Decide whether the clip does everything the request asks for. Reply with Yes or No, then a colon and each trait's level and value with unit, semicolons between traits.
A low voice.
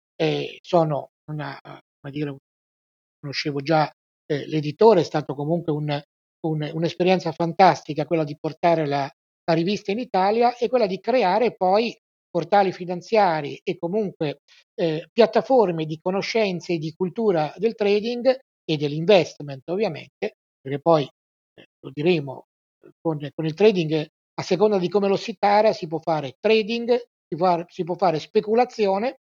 No: medium, 175 Hz